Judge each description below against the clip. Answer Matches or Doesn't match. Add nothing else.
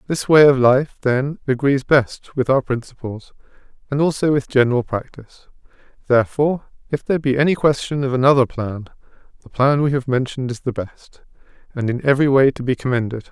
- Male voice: Matches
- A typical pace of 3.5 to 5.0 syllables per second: Doesn't match